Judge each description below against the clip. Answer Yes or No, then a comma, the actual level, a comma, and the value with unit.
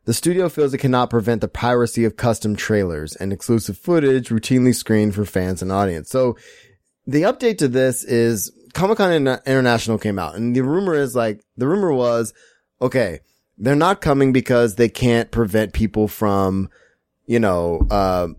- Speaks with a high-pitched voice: No, low, 115 Hz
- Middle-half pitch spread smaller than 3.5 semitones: No, average, 4.0 semitones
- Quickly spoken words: No, average, 175 wpm